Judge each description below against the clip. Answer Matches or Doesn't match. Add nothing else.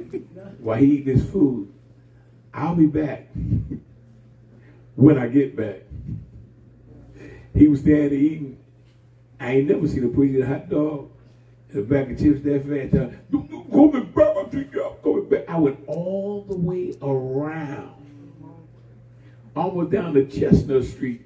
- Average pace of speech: Doesn't match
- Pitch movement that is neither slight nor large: Matches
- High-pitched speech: Doesn't match